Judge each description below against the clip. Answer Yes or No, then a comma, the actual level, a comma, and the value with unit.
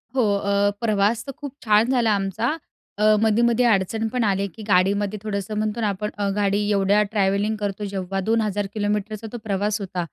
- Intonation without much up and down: Yes, narrow, 1.8 semitones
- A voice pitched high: Yes, high, 210 Hz